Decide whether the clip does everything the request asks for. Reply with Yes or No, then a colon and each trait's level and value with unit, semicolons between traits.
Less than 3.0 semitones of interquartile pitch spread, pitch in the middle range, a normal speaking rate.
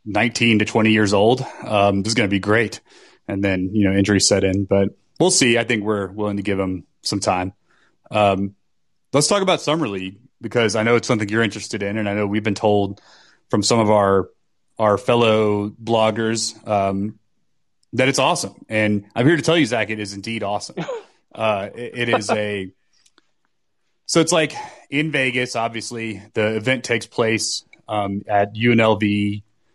No: narrow, 2.6 semitones; low, 110 Hz; average, 185 wpm